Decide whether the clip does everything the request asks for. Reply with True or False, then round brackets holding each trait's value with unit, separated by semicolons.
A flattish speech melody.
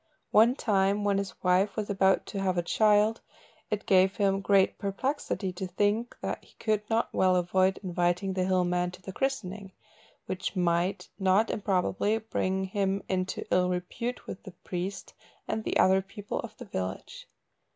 True (2.1 semitones)